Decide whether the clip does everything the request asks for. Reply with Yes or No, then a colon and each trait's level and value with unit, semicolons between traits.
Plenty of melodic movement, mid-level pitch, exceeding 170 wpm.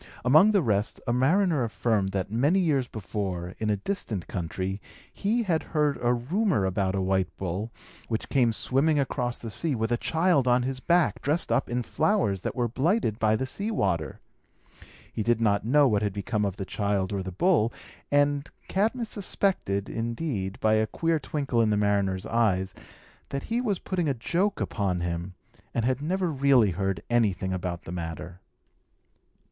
No: wide, 7.3 semitones; low, 115 Hz; average, 180 wpm